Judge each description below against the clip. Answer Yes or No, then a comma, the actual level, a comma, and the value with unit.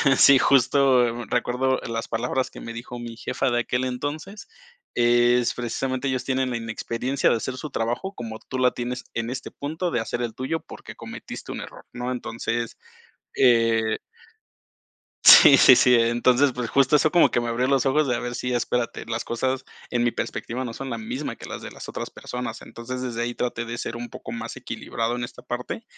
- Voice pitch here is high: No, low, 125 Hz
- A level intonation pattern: Yes, narrow, 1.8 semitones